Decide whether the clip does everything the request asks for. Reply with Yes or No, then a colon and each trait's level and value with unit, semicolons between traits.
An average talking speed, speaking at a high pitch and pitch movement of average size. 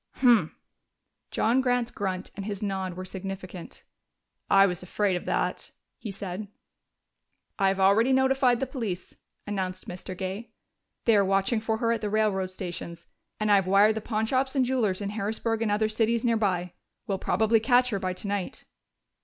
Yes: average, 170 wpm; high, 205 Hz; average, 3.2 semitones